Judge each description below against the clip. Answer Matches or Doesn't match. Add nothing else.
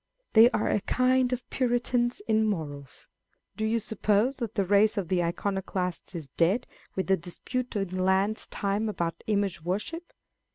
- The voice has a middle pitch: Doesn't match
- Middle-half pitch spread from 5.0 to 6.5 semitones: Doesn't match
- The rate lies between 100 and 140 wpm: Doesn't match